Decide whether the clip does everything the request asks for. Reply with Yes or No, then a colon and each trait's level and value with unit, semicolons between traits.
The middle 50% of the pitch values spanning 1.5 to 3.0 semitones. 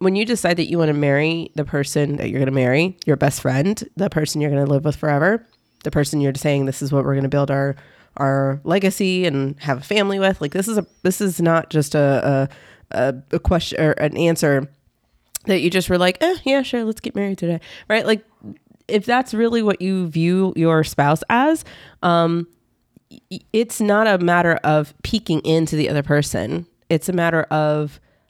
No: average, 5.1 semitones